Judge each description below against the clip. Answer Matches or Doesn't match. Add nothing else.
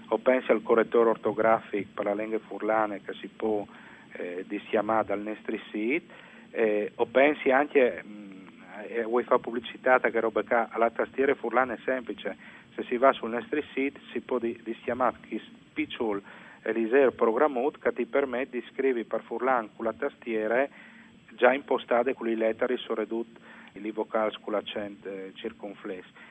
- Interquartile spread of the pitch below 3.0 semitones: Matches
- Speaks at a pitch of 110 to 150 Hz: Matches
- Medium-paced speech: Matches